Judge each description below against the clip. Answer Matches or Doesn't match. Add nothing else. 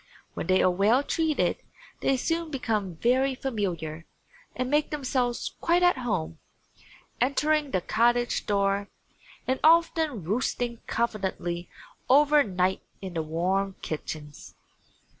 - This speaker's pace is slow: Matches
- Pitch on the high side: Matches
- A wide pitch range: Matches